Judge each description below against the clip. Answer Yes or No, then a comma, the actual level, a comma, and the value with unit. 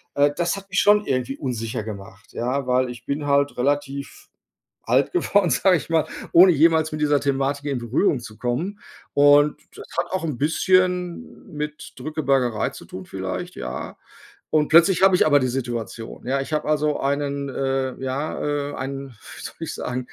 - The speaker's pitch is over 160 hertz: No, medium, 140 Hz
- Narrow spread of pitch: No, average, 3.6 semitones